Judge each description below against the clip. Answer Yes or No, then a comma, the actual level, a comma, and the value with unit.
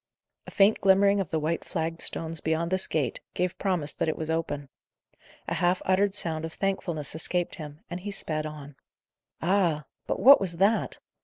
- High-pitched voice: No, medium, 170 Hz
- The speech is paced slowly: No, average, 180 wpm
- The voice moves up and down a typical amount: Yes, average, 3.4 semitones